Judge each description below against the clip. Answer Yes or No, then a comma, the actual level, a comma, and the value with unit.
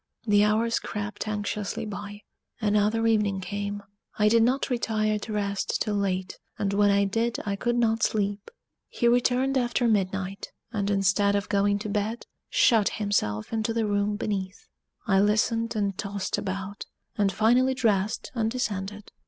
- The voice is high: Yes, high, 210 Hz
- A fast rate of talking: No, average, 155 wpm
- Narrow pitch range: Yes, narrow, 2.0 semitones